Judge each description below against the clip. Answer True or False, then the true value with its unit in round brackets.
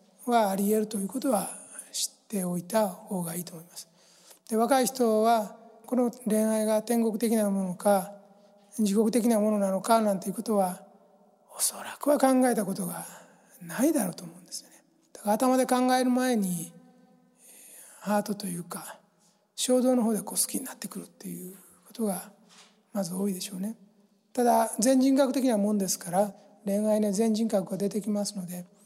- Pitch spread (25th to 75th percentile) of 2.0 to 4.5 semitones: True (2.9 semitones)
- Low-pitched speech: False (210 Hz)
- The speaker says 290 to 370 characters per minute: True (325 characters per minute)